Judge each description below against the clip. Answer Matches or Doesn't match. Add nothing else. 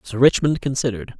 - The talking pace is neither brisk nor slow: Matches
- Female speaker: Doesn't match